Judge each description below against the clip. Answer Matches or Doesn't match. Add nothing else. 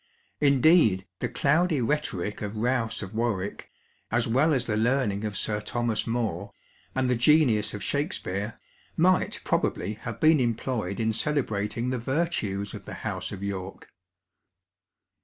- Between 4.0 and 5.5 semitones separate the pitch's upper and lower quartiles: Matches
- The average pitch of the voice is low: Matches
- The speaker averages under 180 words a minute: Matches